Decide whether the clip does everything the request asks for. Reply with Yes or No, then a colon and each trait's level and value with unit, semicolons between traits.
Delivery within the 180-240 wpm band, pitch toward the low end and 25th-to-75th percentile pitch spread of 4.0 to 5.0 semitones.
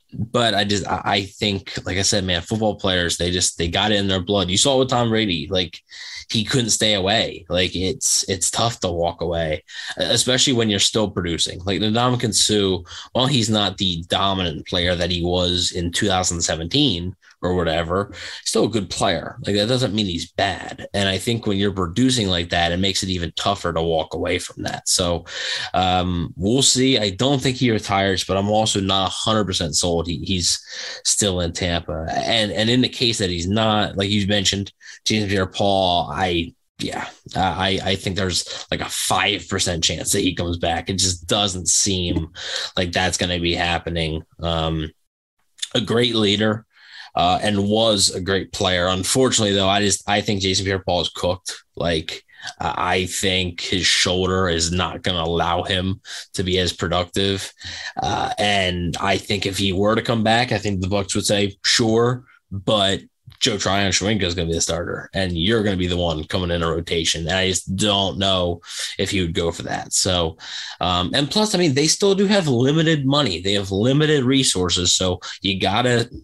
No: average, 195 wpm; very low, 95 Hz; average, 3.1 semitones